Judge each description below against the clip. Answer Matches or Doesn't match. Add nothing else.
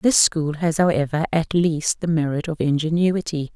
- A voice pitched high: Doesn't match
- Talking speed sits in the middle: Matches